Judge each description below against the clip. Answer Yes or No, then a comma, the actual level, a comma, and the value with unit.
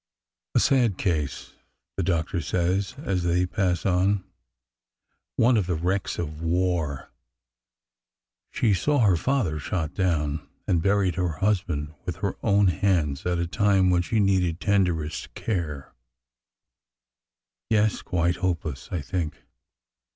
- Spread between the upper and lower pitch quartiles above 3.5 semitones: No, average, 3.2 semitones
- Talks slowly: Yes, slow, 130 wpm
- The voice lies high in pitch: No, very low, 90 Hz